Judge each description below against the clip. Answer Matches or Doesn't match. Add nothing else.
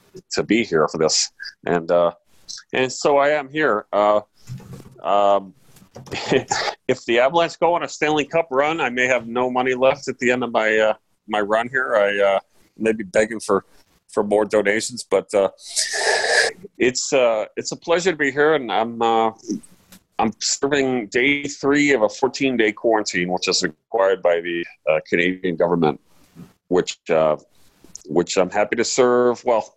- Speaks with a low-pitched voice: Matches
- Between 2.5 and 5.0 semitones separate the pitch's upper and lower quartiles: Doesn't match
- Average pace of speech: Matches